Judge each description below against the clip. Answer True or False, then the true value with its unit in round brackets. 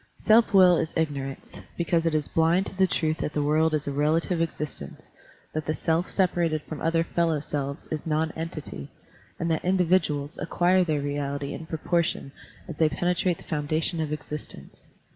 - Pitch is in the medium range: True (160 Hz)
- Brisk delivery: False (175 wpm)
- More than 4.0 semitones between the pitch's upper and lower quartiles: False (2.4 semitones)